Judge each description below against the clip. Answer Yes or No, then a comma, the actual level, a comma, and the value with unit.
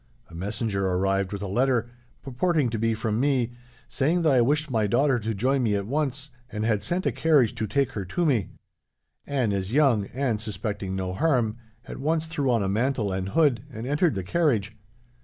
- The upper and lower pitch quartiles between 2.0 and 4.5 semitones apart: No, average, 5.3 semitones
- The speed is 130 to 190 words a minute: No, average, 200 wpm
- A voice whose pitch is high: No, low, 120 Hz